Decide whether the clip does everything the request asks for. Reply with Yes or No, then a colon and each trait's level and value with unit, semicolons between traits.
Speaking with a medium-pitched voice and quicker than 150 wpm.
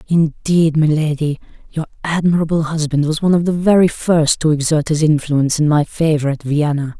Yes: medium, 155 Hz; average, 170 wpm